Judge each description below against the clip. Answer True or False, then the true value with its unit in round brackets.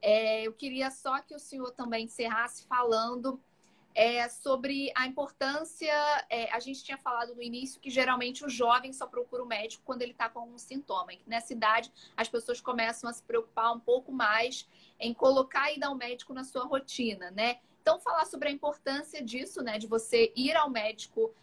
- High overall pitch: True (250 Hz)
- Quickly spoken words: True (190 wpm)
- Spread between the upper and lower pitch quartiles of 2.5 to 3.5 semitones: True (2.9 semitones)